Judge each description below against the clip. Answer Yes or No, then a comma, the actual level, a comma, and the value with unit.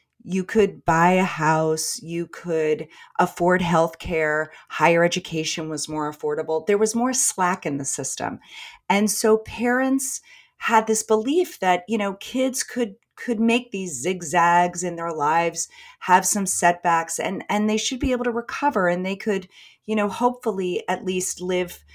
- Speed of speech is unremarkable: Yes, average, 165 wpm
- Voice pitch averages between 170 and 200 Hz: Yes, medium, 185 Hz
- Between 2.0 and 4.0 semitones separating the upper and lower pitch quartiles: No, average, 4.8 semitones